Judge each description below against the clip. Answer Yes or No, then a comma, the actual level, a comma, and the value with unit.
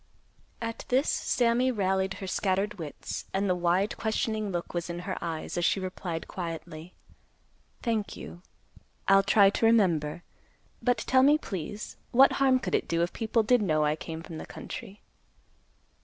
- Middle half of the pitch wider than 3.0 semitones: Yes, average, 4.6 semitones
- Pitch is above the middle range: Yes, high, 195 Hz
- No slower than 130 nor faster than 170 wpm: Yes, average, 165 wpm